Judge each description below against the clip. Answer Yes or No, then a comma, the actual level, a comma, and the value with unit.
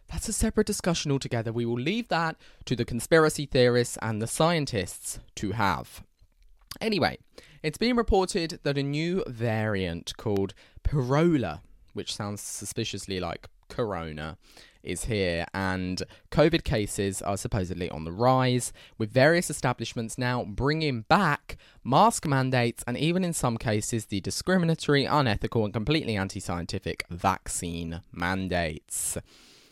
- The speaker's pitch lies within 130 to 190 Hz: No, low, 115 Hz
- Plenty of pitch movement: Yes, wide, 7.4 semitones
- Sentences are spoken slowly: Yes, slow, 130 wpm